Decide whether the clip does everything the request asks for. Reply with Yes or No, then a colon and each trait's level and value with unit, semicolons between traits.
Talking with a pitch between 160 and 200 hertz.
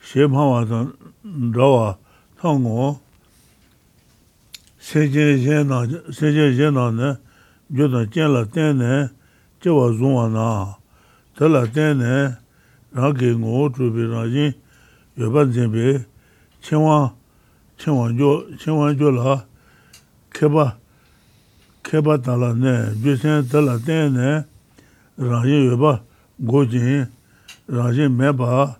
No: low, 135 Hz